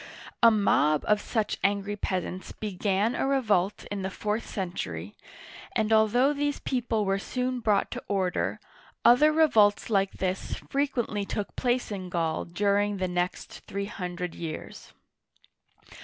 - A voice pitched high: Yes, high, 205 Hz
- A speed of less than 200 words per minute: Yes, average, 140 wpm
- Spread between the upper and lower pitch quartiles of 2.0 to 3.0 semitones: No, average, 3.6 semitones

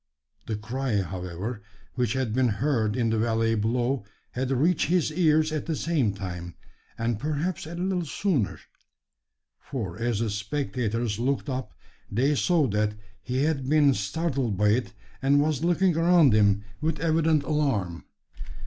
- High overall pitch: No, low, 130 Hz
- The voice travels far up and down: Yes, wide, 6.2 semitones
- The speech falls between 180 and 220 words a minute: No, average, 150 wpm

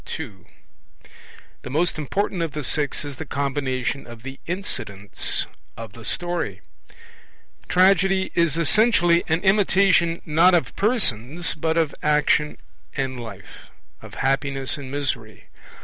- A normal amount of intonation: Yes, average, 4.7 semitones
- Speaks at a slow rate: Yes, slow, 125 wpm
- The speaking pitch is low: No, medium, 150 Hz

